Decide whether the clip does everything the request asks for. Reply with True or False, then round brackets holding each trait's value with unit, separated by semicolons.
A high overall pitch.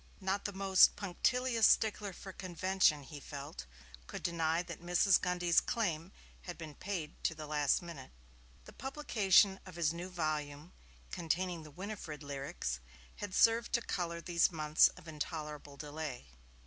False (170 Hz)